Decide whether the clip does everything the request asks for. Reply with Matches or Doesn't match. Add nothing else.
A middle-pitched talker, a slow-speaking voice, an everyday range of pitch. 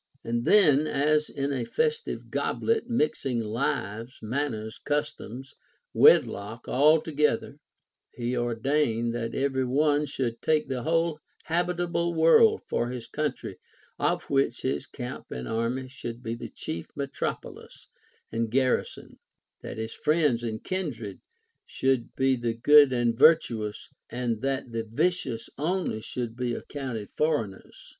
Doesn't match